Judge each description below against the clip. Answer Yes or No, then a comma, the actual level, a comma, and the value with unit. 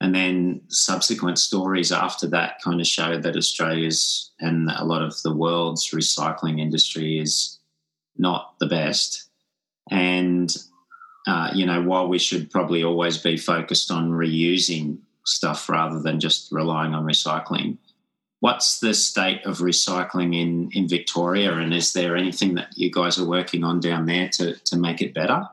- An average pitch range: No, narrow, 2.0 semitones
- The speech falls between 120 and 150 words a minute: No, average, 160 wpm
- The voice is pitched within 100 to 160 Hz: No, very low, 85 Hz